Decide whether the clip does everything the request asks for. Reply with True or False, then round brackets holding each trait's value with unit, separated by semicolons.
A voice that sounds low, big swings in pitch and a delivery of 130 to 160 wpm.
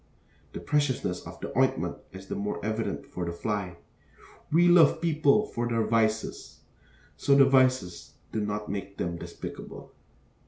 True (110 Hz; 5.8 semitones; 150 wpm)